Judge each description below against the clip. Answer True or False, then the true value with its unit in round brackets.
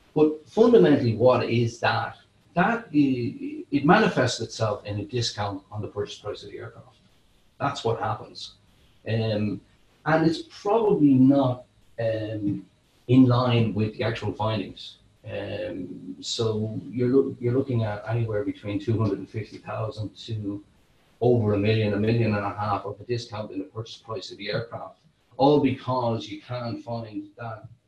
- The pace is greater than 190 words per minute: False (155 wpm)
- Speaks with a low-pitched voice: True (115 Hz)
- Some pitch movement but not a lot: True (3.8 semitones)